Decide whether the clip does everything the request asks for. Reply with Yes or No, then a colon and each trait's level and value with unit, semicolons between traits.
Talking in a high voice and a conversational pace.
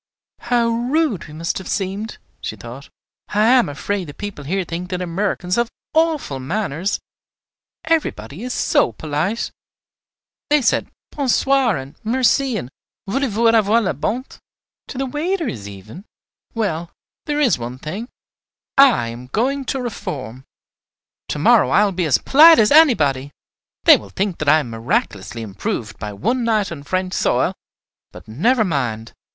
Yes: high, 195 Hz; average, 155 wpm